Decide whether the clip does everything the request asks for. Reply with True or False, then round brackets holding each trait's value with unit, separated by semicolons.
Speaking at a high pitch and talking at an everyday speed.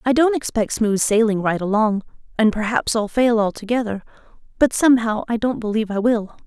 True (225 Hz; 175 wpm)